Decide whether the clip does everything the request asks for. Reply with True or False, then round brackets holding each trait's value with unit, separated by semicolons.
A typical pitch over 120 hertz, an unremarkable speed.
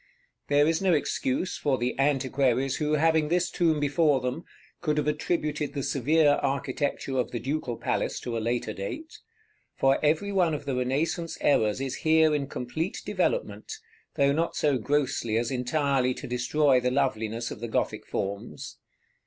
True (140 Hz; 165 wpm)